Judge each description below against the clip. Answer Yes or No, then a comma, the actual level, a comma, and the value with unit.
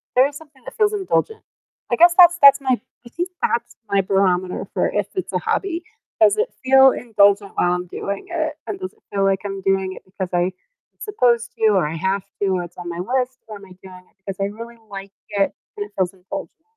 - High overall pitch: Yes, high, 205 Hz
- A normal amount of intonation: No, wide, 6.4 semitones